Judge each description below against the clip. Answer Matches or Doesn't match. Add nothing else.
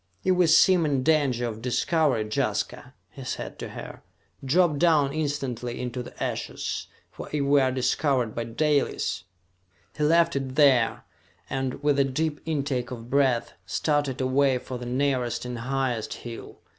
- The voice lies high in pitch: Doesn't match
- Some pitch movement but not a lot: Matches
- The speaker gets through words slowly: Doesn't match